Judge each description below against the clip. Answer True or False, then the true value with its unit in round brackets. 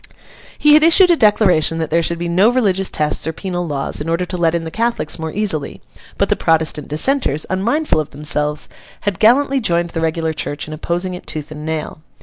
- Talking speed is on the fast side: True (210 wpm)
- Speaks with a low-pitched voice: False (170 Hz)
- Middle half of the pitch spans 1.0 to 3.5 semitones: False (5.0 semitones)